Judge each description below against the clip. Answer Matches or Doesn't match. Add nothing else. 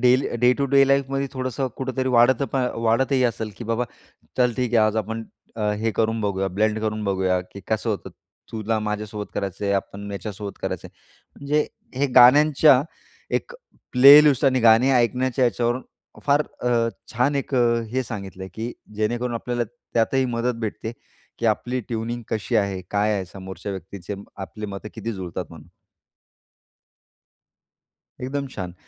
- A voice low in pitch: Matches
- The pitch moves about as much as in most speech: Matches